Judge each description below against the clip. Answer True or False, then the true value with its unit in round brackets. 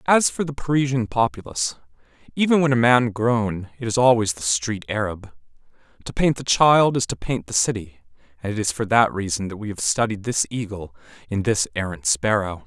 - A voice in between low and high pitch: False (110 Hz)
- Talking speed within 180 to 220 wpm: True (195 wpm)